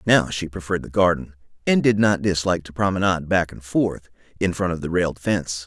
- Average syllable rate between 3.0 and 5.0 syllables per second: No, 6.1 syllables/s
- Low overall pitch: Yes, very low, 90 Hz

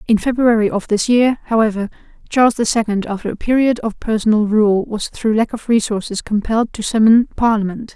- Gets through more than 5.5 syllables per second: Yes, 5.7 syllables/s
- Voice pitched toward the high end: Yes, high, 220 Hz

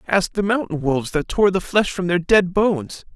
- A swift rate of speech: Yes, fast, 230 wpm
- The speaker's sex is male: Yes, male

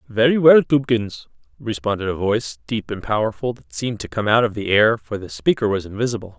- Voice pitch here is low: Yes, low, 110 Hz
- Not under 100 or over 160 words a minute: No, fast, 205 wpm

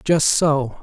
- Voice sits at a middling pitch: Yes, medium, 150 Hz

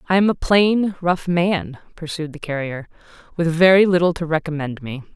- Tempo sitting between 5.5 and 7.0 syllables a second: No, 5.0 syllables/s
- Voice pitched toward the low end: No, medium, 165 Hz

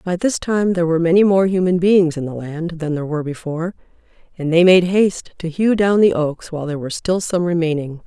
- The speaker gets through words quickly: Yes, fast, 230 wpm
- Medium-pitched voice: Yes, medium, 170 Hz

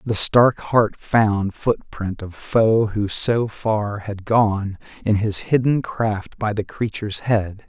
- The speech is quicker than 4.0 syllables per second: No, 3.3 syllables/s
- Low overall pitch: Yes, low, 105 Hz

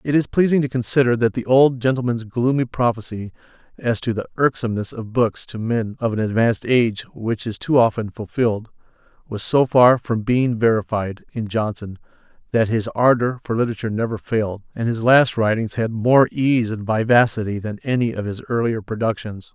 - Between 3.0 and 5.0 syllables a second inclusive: No, 5.4 syllables/s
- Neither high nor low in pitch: No, low, 115 Hz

